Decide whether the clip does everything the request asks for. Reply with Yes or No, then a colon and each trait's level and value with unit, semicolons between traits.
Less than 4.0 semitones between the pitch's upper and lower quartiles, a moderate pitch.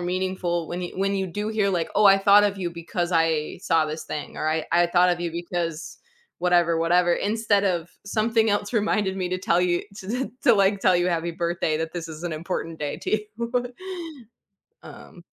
Yes: average, 2.8 semitones; medium, 180 Hz